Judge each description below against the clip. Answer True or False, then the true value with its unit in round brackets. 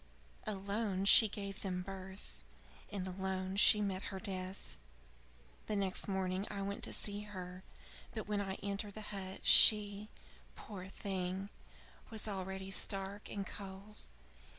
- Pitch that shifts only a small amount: True (1.4 semitones)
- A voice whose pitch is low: False (195 Hz)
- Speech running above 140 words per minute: False (135 wpm)